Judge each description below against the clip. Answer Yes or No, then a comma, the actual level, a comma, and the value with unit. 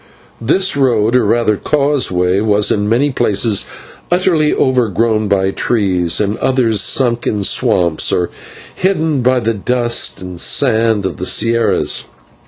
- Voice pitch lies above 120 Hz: No, low, 115 Hz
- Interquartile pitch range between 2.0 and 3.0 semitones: No, average, 4.1 semitones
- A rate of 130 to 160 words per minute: Yes, average, 140 wpm